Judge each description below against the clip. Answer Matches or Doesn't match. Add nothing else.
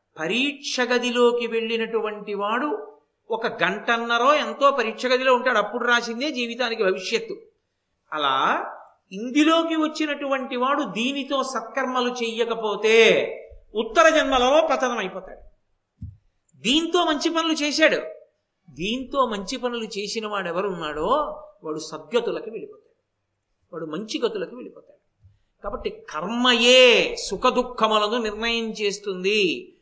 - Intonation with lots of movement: Matches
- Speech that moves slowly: Doesn't match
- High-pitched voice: Matches